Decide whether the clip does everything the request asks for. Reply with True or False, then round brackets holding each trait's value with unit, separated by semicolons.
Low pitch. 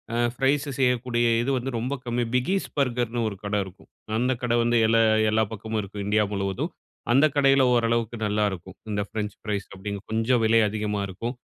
True (115 Hz)